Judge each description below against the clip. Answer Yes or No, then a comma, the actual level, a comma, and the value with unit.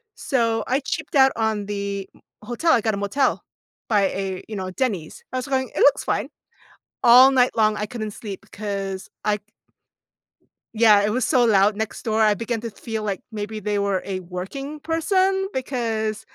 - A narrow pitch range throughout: No, average, 3.9 semitones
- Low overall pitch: No, high, 220 Hz